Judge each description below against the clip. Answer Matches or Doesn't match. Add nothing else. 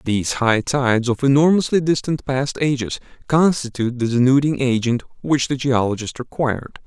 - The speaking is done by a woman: Doesn't match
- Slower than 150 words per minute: Matches